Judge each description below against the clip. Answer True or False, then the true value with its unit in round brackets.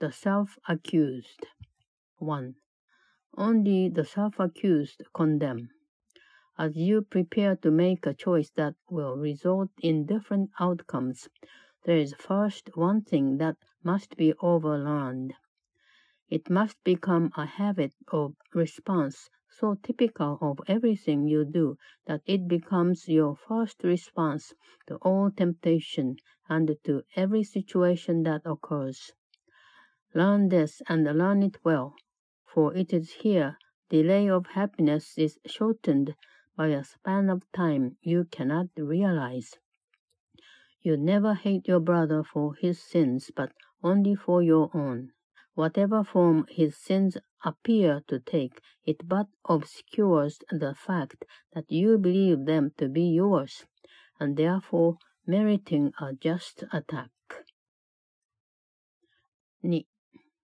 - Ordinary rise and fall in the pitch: True (4.2 semitones)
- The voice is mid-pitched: True (170 Hz)